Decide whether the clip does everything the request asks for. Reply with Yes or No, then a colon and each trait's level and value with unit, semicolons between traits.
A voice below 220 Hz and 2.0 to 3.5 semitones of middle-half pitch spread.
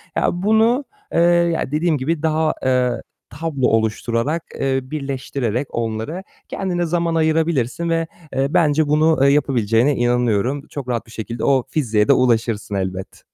No: medium, 140 Hz; average, 5.3 semitones